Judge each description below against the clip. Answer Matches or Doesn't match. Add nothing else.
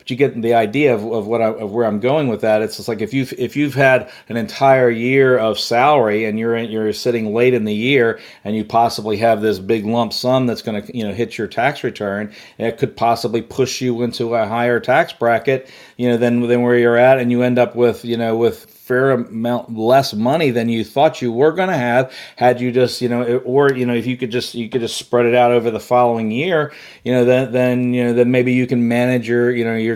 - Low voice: Matches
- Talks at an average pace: Doesn't match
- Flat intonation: Matches